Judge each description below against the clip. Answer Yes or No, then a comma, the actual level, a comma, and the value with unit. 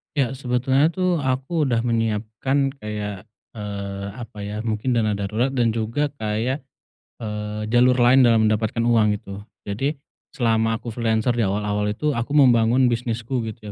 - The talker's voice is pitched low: Yes, low, 115 Hz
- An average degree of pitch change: Yes, average, 3.2 semitones